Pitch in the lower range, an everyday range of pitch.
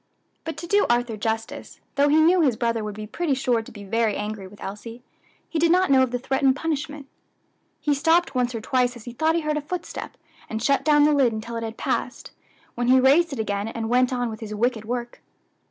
No: very high, 250 Hz; average, 4.7 semitones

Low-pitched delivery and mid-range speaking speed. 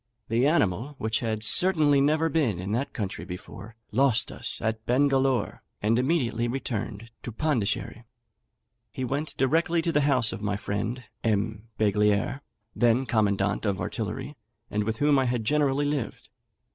Yes: low, 120 Hz; average, 150 wpm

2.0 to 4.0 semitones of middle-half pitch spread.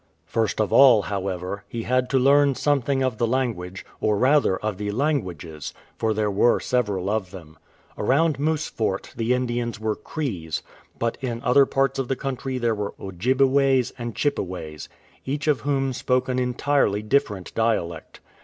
No: average, 4.8 semitones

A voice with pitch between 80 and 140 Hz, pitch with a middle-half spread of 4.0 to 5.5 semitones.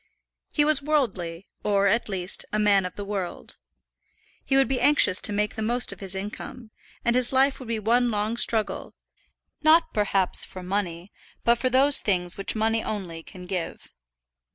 No: high, 210 Hz; average, 4.3 semitones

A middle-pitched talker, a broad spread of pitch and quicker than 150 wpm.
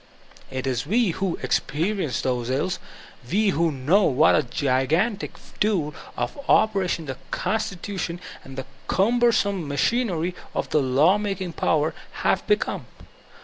No: medium, 170 Hz; wide, 6.1 semitones; slow, 135 wpm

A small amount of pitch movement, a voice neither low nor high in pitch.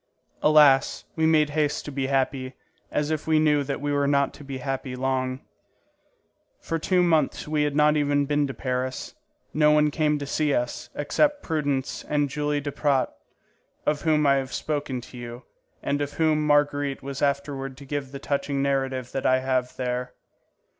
Yes: narrow, 2.0 semitones; medium, 145 Hz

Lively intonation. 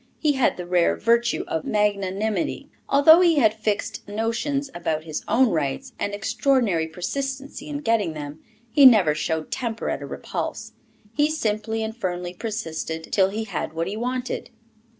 Yes: wide, 6.4 semitones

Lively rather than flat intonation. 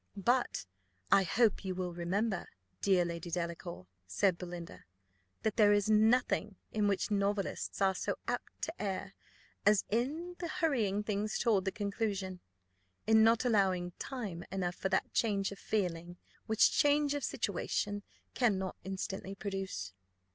No: average, 2.9 semitones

